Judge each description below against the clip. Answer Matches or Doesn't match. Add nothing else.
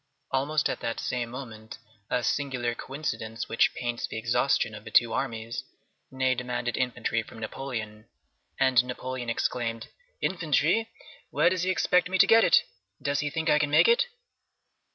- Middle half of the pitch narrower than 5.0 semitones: Matches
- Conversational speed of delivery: Matches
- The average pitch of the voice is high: Doesn't match